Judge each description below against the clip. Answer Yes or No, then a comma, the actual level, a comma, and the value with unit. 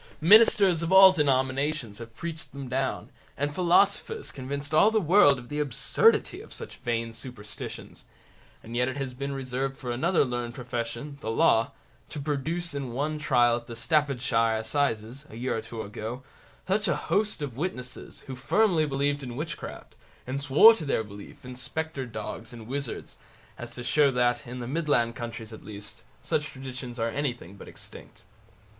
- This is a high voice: No, low, 130 Hz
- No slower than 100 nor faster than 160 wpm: No, average, 175 wpm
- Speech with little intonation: No, average, 4.1 semitones